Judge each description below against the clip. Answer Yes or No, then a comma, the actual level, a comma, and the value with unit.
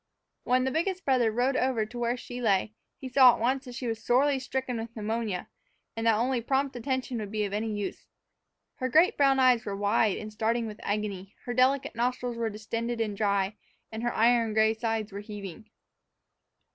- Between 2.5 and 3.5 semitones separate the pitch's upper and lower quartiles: Yes, average, 3.0 semitones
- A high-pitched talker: Yes, high, 230 Hz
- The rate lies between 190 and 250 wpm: Yes, average, 195 wpm